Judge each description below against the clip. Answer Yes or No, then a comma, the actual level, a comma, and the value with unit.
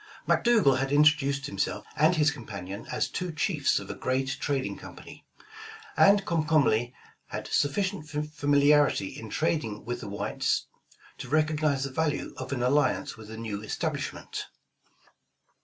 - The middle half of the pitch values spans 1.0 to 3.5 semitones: No, average, 4.0 semitones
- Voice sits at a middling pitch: Yes, medium, 145 Hz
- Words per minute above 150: No, average, 140 wpm